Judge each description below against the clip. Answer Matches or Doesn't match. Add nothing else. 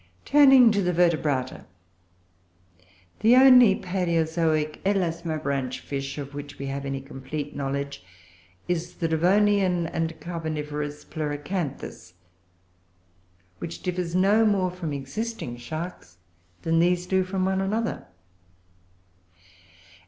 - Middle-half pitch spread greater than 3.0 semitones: Matches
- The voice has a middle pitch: Matches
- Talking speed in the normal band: Doesn't match